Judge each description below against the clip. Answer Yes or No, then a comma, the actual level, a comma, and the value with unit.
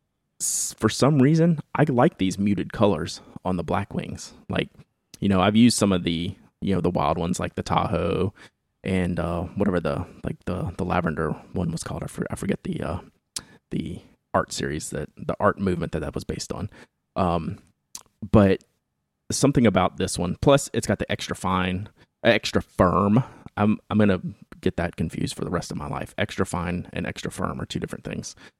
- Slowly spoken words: No, average, 195 wpm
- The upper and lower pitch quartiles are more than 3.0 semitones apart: Yes, average, 3.4 semitones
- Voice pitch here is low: Yes, low, 100 Hz